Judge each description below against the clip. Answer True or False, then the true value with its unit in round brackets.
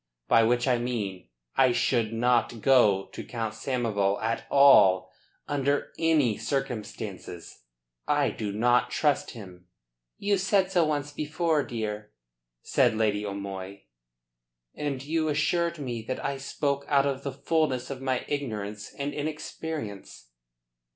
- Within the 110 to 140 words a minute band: True (135 wpm)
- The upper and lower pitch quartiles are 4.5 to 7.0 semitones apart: True (5.4 semitones)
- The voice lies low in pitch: True (125 Hz)